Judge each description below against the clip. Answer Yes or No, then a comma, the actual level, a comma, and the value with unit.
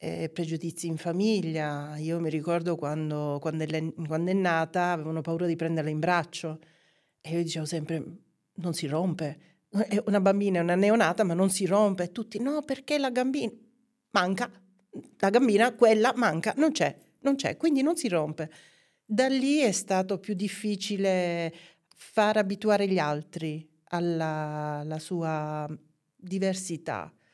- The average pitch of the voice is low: No, medium, 175 Hz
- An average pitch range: Yes, average, 4.6 semitones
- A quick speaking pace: No, average, 145 wpm